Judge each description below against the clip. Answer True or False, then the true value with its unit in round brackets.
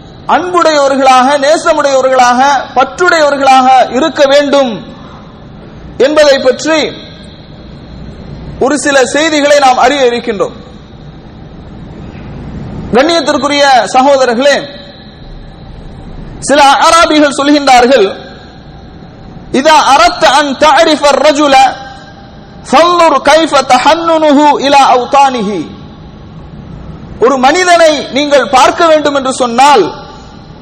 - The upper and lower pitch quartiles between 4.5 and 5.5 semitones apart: False (2.9 semitones)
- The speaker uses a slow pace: True (45 wpm)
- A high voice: True (285 Hz)